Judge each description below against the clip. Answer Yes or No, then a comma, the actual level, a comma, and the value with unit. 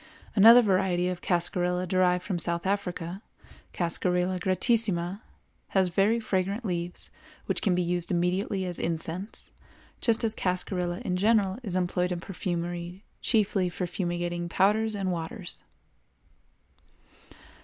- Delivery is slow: Yes, slow, 120 wpm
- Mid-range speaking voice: Yes, medium, 180 Hz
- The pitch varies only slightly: Yes, narrow, 2.1 semitones